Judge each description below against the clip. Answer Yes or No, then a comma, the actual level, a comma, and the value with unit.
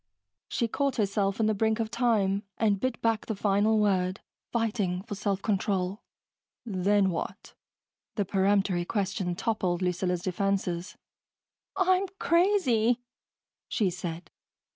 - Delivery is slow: Yes, slow, 120 wpm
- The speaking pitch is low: No, high, 200 Hz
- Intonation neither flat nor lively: Yes, average, 3.2 semitones